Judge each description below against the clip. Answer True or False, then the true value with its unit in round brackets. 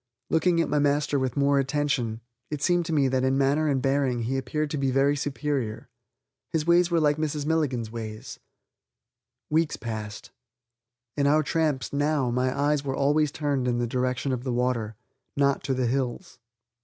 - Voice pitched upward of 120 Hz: True (140 Hz)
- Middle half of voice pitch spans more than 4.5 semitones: False (2.8 semitones)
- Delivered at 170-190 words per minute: True (180 wpm)